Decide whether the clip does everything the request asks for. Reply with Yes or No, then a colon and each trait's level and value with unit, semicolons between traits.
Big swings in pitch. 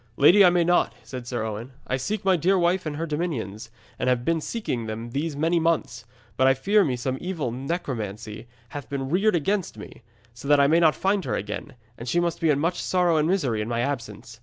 Yes: wide, 6.3 semitones